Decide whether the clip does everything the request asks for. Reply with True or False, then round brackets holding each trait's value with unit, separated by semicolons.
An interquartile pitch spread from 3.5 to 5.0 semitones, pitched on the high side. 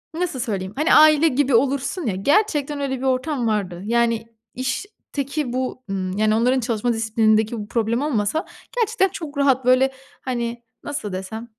True (4.5 semitones; 250 Hz)